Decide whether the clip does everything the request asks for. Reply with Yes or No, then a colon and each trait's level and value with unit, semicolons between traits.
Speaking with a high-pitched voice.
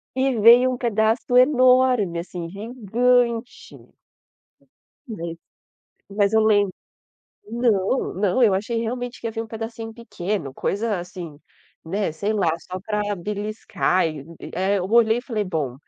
Yes: high, 215 Hz